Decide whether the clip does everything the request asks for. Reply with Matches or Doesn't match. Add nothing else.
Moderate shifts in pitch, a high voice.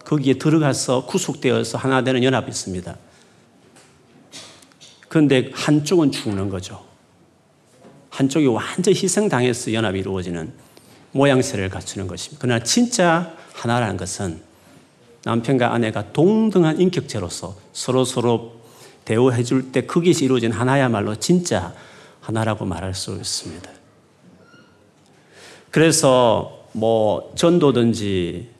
Doesn't match